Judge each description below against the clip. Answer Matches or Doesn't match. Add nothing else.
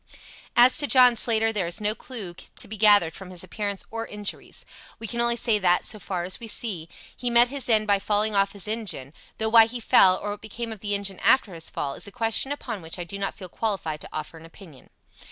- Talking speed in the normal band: Doesn't match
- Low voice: Doesn't match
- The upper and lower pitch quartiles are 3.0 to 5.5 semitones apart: Matches